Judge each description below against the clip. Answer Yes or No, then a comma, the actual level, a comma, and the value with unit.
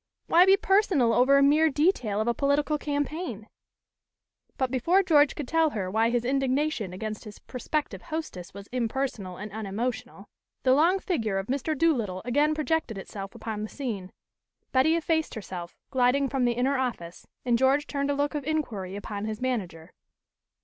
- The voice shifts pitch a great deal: Yes, wide, 5.7 semitones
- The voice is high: Yes, very high, 255 Hz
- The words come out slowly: No, average, 170 wpm